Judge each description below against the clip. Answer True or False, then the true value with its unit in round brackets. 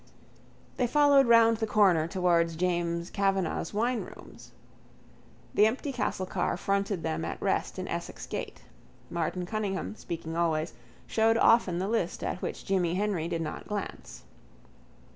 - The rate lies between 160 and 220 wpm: False (140 wpm)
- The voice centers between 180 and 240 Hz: True (190 Hz)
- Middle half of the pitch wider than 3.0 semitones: True (4.5 semitones)